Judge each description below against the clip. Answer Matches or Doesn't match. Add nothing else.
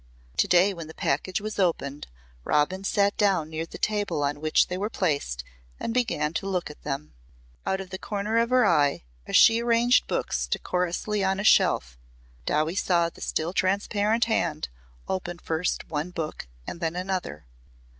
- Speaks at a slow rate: Doesn't match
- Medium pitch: Matches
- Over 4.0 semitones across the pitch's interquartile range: Matches